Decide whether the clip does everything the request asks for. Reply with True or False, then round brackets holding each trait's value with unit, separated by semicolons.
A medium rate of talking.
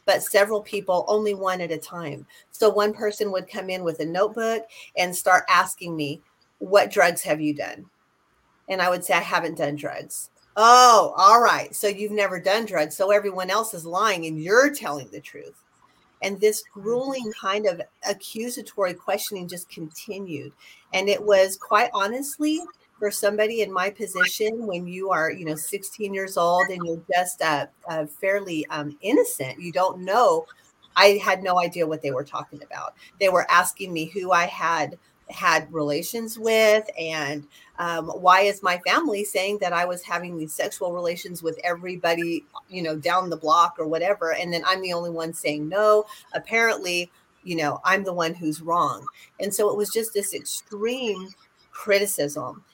True (175 wpm)